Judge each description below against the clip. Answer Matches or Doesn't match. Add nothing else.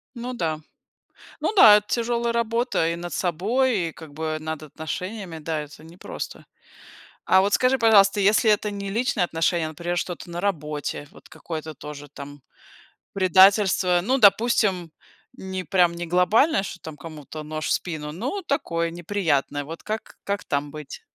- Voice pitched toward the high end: Doesn't match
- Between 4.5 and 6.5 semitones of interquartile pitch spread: Matches